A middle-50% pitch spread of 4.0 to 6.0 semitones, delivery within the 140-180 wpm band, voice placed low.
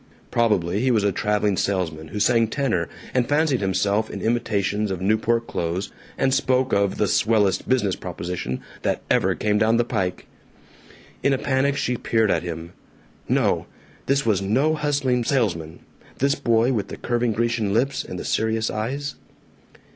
Yes: average, 4.3 semitones; average, 160 wpm; low, 110 Hz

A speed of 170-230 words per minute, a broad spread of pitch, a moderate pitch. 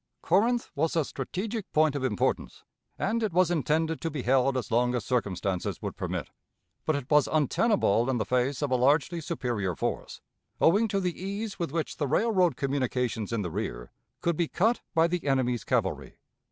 Yes: average, 185 wpm; wide, 6.0 semitones; medium, 145 Hz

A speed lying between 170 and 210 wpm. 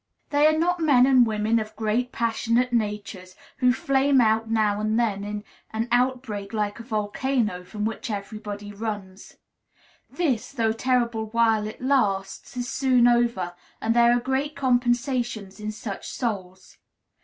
No: average, 150 wpm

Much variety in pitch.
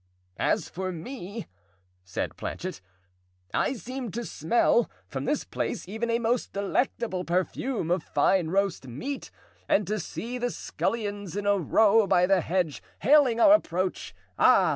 No: average, 4.5 semitones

